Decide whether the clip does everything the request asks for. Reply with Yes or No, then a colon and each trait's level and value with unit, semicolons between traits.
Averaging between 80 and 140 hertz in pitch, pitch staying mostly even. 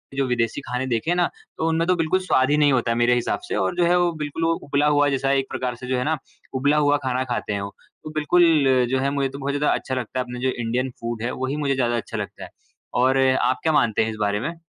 No: low, 135 Hz; average, 3.3 semitones